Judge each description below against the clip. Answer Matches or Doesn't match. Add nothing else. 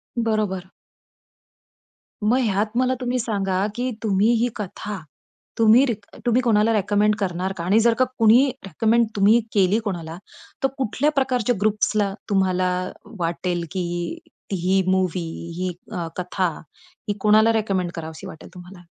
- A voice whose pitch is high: Matches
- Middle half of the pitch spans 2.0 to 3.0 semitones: Doesn't match